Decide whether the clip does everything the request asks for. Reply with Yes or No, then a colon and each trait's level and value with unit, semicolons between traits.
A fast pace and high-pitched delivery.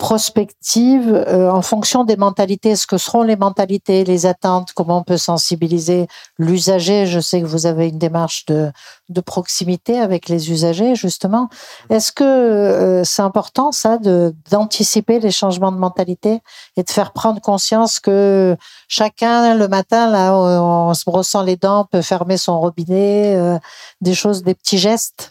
No: average, 165 wpm; high, 195 Hz